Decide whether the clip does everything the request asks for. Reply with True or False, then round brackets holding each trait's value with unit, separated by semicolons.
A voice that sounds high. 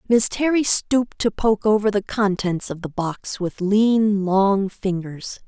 True (205 Hz)